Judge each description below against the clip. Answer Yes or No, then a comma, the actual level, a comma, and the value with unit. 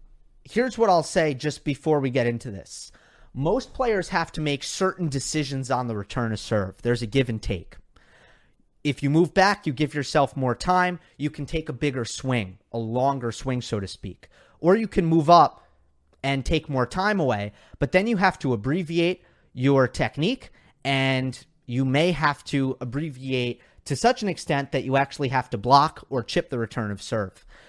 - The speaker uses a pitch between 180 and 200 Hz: No, low, 135 Hz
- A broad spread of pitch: No, average, 4.4 semitones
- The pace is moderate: Yes, average, 190 wpm